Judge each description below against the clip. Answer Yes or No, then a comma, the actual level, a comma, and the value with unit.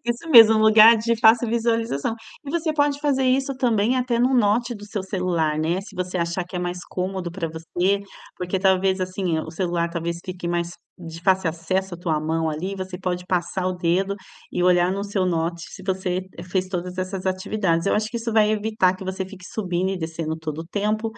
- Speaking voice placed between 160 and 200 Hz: Yes, medium, 185 Hz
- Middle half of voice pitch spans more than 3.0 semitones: Yes, average, 3.7 semitones